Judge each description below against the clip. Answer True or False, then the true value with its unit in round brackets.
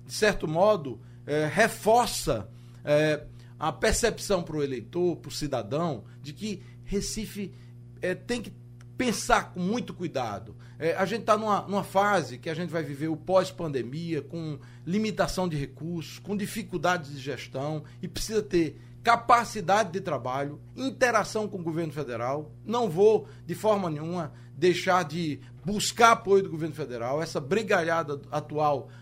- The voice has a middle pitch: True (165 Hz)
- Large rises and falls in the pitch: True (6.4 semitones)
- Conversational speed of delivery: True (150 wpm)